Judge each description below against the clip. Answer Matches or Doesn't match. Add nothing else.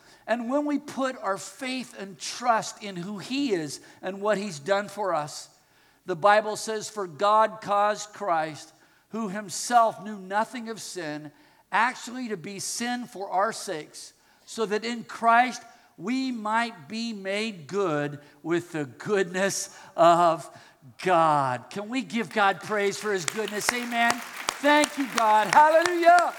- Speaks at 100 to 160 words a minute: Matches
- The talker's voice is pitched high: Matches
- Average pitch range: Matches